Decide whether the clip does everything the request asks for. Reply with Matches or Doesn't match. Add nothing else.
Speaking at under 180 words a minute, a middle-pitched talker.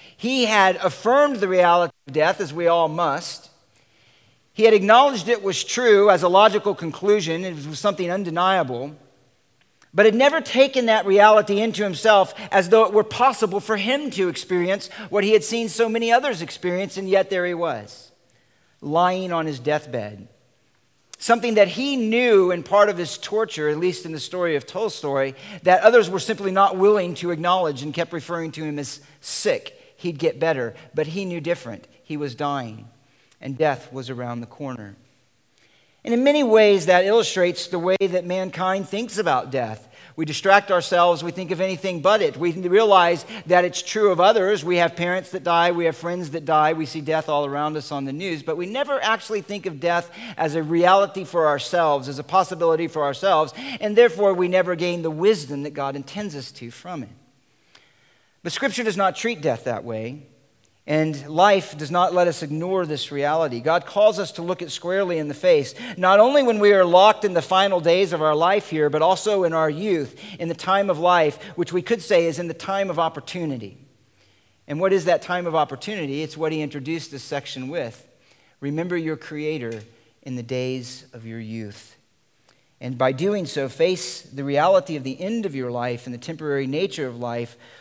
Doesn't match